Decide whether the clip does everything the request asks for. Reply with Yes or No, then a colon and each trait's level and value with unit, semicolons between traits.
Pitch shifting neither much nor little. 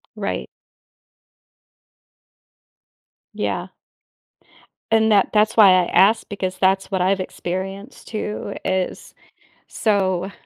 No: narrow, 2.0 semitones